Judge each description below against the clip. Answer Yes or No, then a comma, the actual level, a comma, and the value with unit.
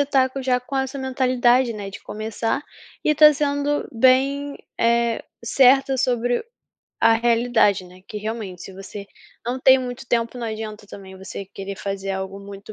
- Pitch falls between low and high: No, high, 235 Hz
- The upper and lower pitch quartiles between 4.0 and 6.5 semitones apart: Yes, average, 4.4 semitones